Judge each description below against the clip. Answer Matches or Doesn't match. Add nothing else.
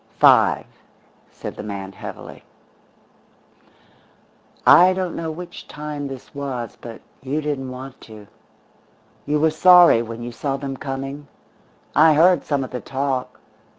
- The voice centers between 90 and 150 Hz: Matches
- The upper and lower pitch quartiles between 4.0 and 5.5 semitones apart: Doesn't match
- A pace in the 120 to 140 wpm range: Matches